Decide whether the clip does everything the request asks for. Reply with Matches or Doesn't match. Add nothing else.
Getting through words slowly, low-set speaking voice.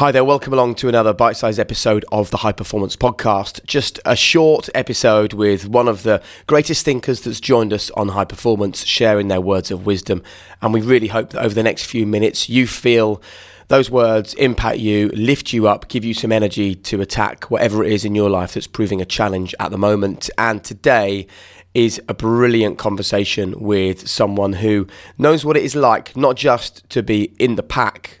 Doesn't match